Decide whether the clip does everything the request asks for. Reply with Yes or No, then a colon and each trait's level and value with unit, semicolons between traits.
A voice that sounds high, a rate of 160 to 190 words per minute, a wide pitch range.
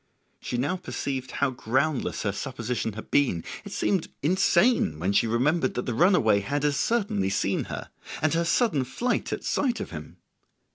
No: low, 135 Hz; average, 175 wpm; wide, 7.2 semitones